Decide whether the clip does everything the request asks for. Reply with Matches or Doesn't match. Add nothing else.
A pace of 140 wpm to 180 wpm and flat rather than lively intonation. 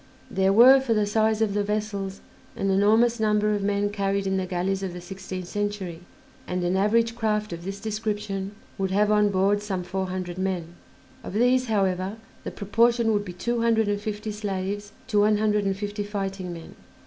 Doesn't match